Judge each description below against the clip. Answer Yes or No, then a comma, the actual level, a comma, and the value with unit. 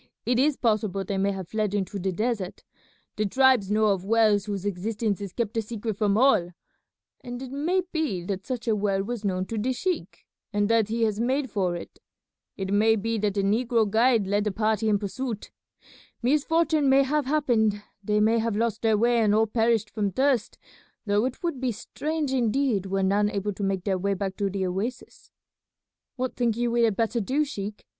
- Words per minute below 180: No, fast, 205 wpm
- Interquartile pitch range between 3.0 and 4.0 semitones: Yes, average, 3.3 semitones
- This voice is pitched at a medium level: No, high, 220 Hz